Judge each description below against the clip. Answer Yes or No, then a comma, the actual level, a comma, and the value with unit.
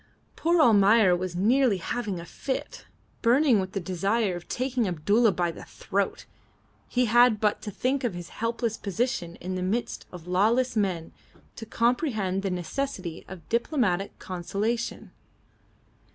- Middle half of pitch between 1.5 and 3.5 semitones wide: No, average, 4.7 semitones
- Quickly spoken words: No, average, 145 wpm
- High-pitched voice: Yes, high, 210 Hz